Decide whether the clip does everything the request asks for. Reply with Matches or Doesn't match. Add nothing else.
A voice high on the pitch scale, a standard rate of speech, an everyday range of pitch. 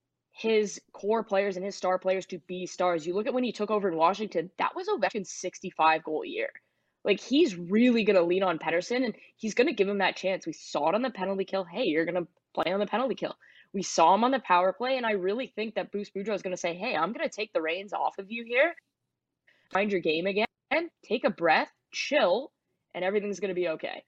Doesn't match